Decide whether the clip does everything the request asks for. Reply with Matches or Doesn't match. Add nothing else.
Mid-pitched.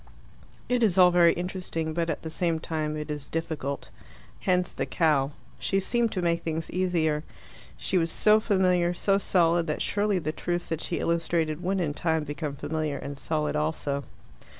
Matches